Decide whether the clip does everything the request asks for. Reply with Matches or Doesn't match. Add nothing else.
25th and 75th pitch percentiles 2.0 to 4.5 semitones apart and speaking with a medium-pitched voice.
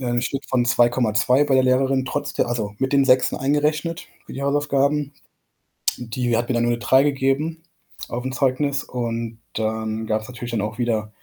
Doesn't match